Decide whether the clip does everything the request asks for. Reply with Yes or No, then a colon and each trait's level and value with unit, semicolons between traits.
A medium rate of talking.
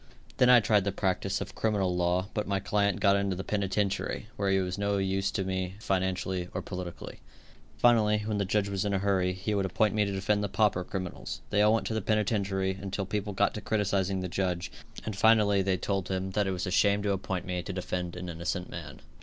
No: fast, 230 wpm